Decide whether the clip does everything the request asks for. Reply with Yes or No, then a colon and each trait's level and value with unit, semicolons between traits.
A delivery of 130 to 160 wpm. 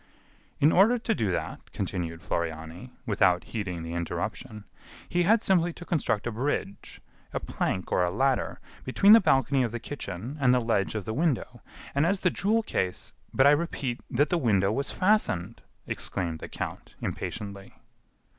No: average, 175 wpm